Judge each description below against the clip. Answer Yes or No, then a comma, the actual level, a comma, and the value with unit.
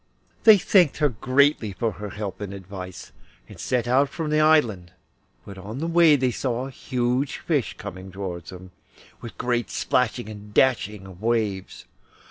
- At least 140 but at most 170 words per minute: Yes, average, 165 wpm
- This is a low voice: Yes, low, 115 Hz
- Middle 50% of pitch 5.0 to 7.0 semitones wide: Yes, wide, 5.4 semitones